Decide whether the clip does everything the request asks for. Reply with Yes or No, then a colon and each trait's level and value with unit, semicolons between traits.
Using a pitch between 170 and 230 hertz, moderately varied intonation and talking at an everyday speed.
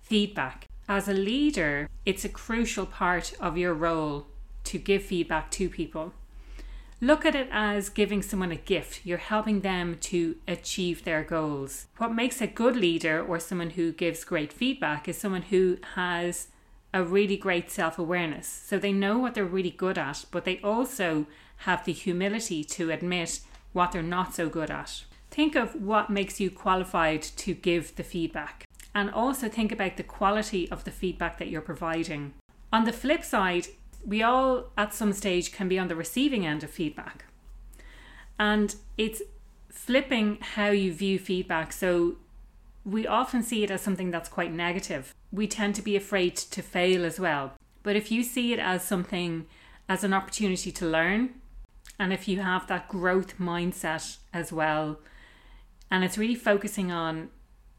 Yes: medium, 185 Hz; average, 3.4 semitones; average, 170 wpm